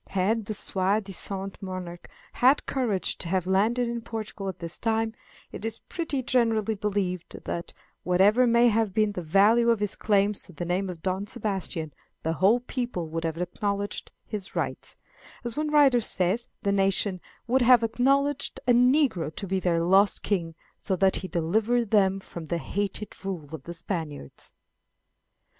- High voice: Yes, high, 200 Hz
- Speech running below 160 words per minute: No, average, 170 wpm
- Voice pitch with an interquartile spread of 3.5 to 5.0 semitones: Yes, average, 4.1 semitones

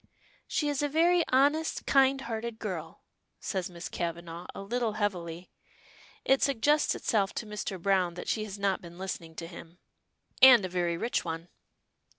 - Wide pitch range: Yes, wide, 6.8 semitones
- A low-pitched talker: No, high, 200 Hz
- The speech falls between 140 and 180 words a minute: Yes, average, 165 wpm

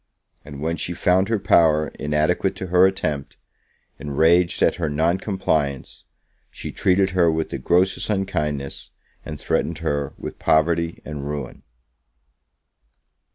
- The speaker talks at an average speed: No, slow, 130 wpm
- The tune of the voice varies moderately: Yes, average, 3.5 semitones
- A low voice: Yes, very low, 80 Hz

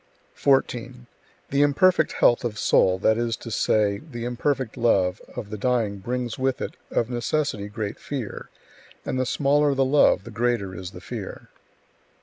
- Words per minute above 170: No, average, 160 wpm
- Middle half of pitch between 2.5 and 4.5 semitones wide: Yes, average, 3.8 semitones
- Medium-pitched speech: No, low, 120 Hz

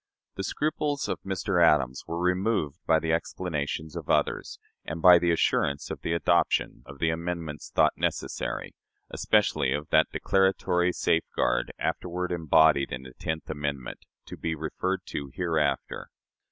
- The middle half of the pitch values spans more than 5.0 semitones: No, average, 3.4 semitones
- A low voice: Yes, very low, 80 Hz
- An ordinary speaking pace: Yes, average, 145 wpm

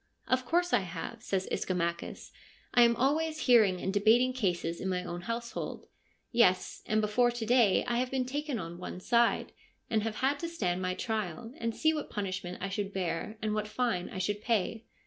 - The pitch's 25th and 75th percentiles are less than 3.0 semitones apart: No, average, 4.9 semitones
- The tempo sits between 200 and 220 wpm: Yes, fast, 205 wpm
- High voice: Yes, high, 215 Hz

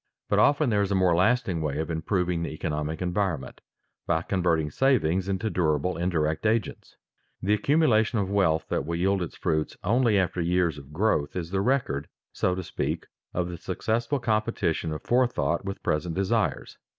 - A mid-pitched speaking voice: No, very low, 90 Hz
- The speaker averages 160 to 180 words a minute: Yes, average, 175 wpm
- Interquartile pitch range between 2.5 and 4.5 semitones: No, average, 4.9 semitones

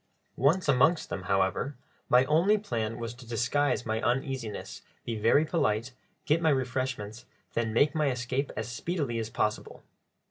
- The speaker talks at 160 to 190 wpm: No, average, 150 wpm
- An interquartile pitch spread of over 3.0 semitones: Yes, average, 4.3 semitones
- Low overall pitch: Yes, low, 125 Hz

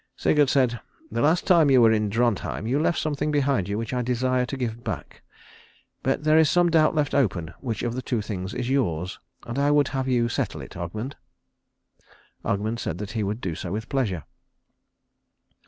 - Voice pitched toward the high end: No, low, 125 Hz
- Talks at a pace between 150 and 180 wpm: No, average, 190 wpm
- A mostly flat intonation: No, average, 4.6 semitones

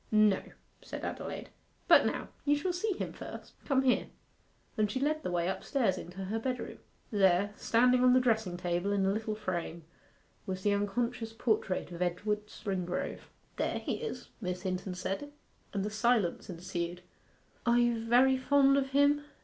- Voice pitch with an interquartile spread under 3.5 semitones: No, average, 5.2 semitones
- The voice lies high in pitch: Yes, high, 215 Hz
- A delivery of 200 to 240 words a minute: No, average, 165 wpm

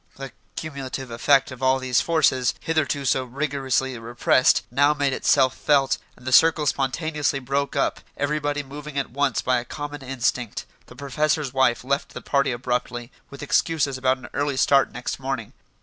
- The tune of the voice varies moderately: No, narrow, 1.9 semitones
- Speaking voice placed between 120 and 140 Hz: Yes, low, 135 Hz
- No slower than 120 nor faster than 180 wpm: Yes, average, 165 wpm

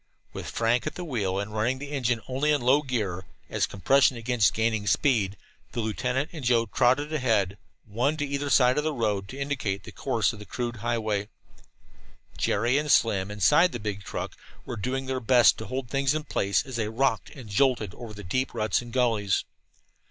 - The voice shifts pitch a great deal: No, average, 4.1 semitones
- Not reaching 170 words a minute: No, average, 195 wpm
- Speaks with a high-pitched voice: No, low, 120 Hz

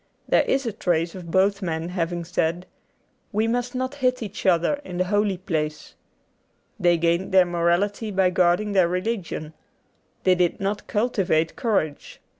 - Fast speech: No, average, 155 wpm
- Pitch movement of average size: Yes, average, 3.4 semitones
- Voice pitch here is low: No, medium, 185 Hz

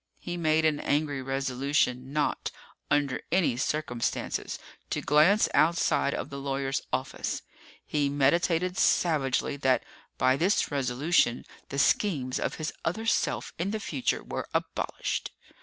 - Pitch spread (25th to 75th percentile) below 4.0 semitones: Yes, average, 3.6 semitones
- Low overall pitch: No, medium, 145 Hz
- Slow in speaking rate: Yes, slow, 130 wpm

